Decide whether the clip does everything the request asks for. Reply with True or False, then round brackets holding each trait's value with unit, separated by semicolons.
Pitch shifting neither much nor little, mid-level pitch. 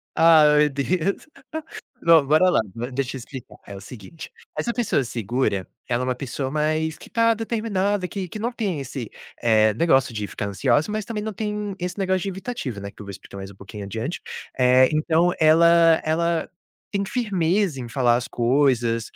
False (7.3 semitones; 155 Hz)